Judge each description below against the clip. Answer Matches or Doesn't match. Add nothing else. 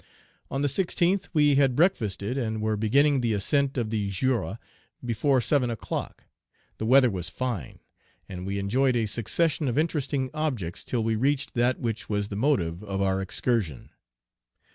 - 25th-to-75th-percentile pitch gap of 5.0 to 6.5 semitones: Matches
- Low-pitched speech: Matches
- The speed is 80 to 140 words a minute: Doesn't match